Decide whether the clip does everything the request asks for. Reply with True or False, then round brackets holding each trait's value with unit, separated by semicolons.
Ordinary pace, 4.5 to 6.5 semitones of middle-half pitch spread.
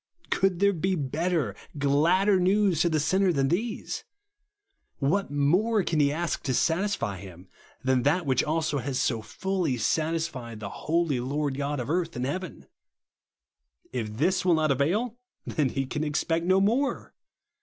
True (155 wpm; 5.2 semitones)